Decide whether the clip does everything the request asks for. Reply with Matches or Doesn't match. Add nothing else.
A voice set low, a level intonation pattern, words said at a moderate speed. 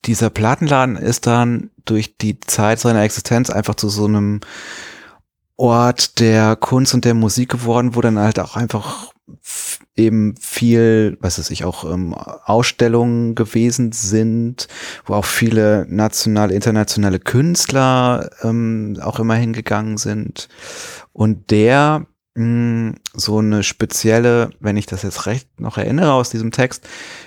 Matches